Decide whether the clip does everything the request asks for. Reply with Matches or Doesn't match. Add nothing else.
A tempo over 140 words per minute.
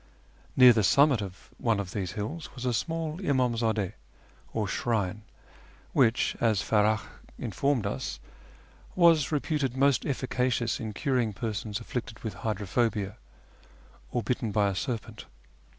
Doesn't match